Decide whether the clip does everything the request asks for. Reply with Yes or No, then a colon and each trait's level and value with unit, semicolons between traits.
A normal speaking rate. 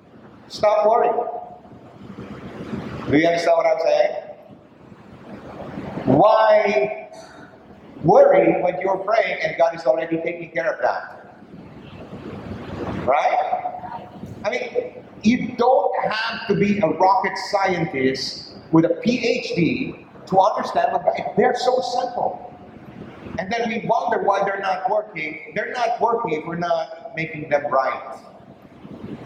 No: slow, 120 wpm